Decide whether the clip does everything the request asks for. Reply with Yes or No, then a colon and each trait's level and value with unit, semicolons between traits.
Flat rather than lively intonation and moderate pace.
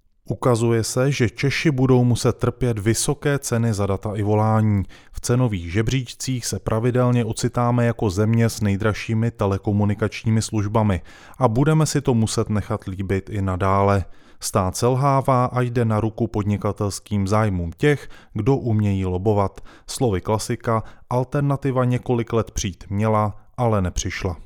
No: average, 3.2 semitones; average, 135 wpm